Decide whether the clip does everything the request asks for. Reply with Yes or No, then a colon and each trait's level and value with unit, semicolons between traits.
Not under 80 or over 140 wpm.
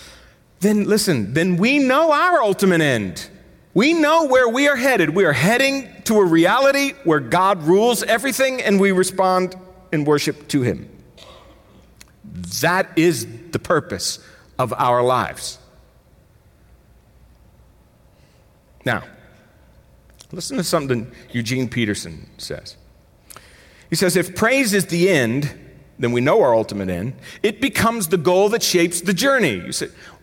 Yes: slow, 135 wpm